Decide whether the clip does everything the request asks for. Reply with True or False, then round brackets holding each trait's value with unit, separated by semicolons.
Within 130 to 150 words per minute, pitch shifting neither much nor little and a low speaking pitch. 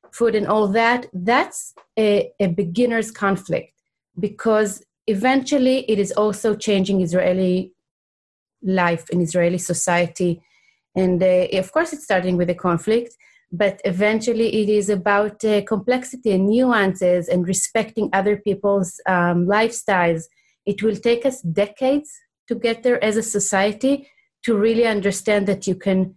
False (140 wpm; 3.6 semitones; 205 Hz)